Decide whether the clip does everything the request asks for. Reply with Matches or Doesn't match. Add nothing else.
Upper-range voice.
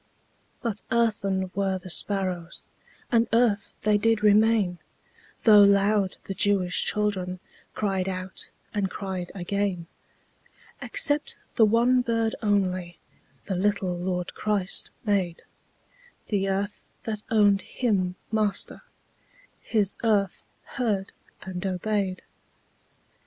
Matches